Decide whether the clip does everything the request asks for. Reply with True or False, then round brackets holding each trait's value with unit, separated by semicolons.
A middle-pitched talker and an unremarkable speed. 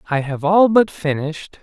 True (170 Hz; 185 wpm)